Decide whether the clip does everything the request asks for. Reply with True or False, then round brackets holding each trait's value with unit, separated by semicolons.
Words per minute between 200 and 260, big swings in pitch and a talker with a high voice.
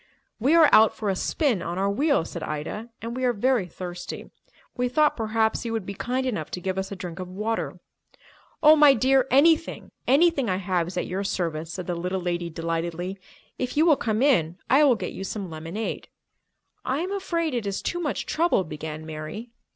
True (205 wpm; 6.8 semitones; 210 Hz)